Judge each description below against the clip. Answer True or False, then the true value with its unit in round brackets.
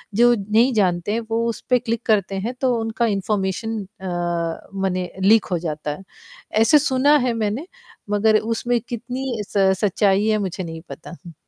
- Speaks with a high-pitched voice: True (215 Hz)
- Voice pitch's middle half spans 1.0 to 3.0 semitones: False (3.7 semitones)